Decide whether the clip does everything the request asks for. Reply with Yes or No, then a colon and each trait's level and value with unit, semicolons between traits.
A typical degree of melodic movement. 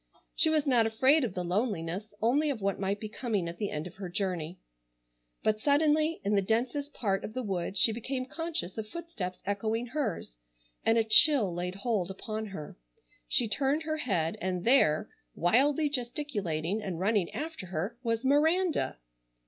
No: wide, 6.6 semitones